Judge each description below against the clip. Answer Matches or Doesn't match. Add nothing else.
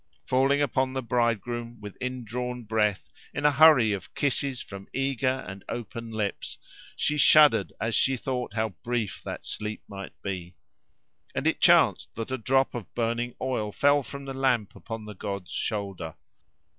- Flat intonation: Doesn't match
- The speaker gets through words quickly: Doesn't match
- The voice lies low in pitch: Matches